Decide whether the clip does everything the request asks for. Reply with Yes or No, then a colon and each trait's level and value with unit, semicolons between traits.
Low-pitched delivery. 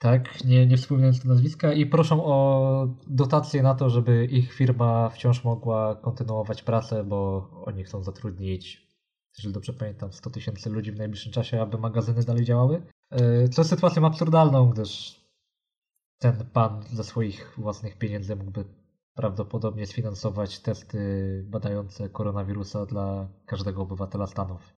Yes: low, 115 Hz